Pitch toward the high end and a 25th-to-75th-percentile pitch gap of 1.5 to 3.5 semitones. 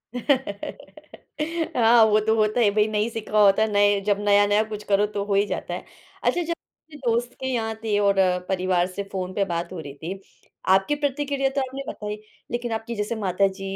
Yes: high, 210 Hz; average, 3.1 semitones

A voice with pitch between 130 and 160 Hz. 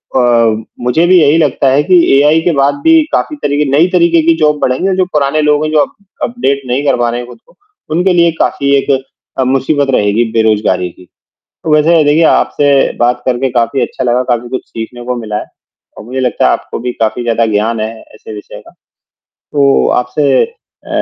Yes: low, 135 Hz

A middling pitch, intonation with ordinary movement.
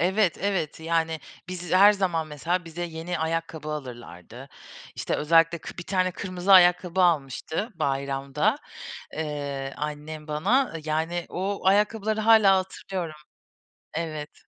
Yes: medium, 165 Hz; average, 3.7 semitones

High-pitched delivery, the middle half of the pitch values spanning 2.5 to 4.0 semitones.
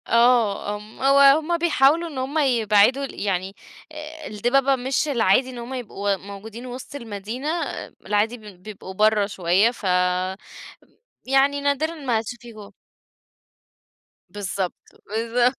No: high, 235 Hz; average, 4.7 semitones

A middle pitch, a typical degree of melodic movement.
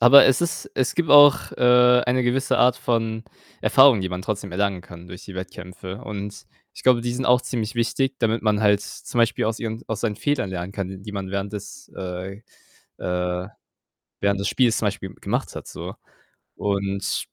No: low, 105 Hz; average, 4.2 semitones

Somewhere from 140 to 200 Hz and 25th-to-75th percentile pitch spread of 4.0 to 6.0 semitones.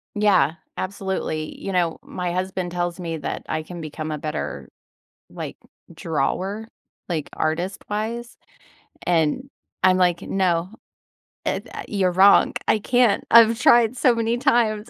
Yes: medium, 185 Hz; average, 4.5 semitones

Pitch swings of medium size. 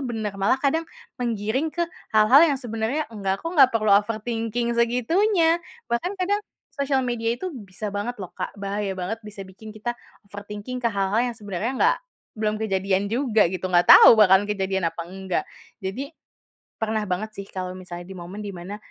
Yes: average, 3.7 semitones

